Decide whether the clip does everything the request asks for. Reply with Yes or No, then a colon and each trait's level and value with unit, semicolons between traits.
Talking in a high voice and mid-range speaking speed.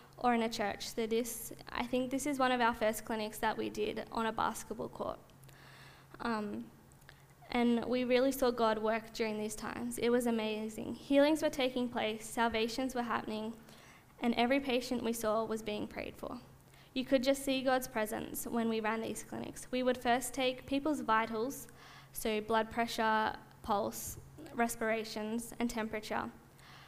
Yes: high, 235 Hz; average, 165 wpm